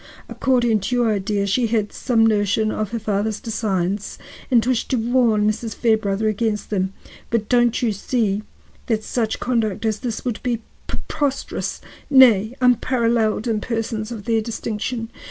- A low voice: No, high, 225 Hz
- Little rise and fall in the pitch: Yes, narrow, 2.2 semitones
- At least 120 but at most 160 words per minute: Yes, average, 155 wpm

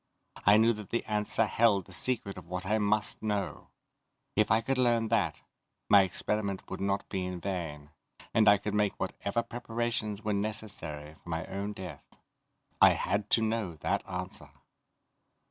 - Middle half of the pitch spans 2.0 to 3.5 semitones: Yes, average, 2.7 semitones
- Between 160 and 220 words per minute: Yes, average, 165 wpm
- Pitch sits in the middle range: No, low, 105 Hz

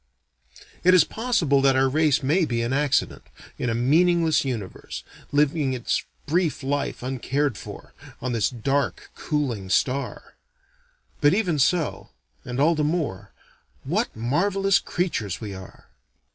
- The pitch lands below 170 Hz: Yes, medium, 140 Hz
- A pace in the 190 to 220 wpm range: No, slow, 135 wpm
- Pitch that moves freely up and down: No, average, 4.7 semitones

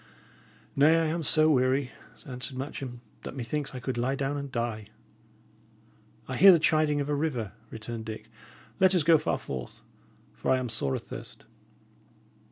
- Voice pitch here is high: No, low, 135 Hz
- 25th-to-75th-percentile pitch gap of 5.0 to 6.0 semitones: No, average, 4.2 semitones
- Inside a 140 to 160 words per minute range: No, average, 170 wpm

